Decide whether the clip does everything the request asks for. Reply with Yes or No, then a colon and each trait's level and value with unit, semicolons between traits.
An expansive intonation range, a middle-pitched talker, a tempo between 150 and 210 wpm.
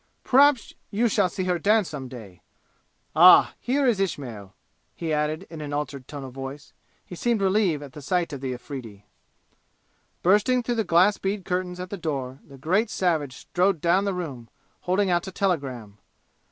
Yes: wide, 6.1 semitones; medium, 170 Hz; average, 175 wpm